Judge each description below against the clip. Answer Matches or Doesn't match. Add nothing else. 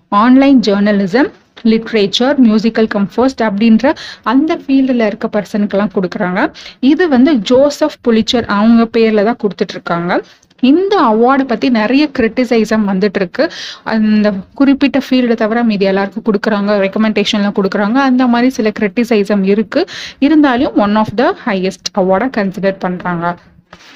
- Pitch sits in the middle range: Doesn't match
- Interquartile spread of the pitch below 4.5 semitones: Matches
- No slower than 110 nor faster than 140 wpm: Matches